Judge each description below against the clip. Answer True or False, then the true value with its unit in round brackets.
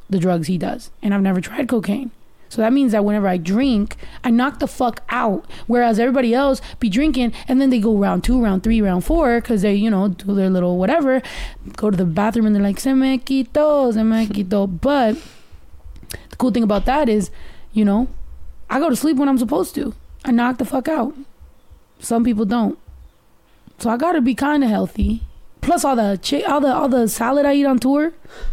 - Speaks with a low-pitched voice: False (235 Hz)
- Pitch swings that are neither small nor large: True (4.7 semitones)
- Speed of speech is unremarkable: False (215 wpm)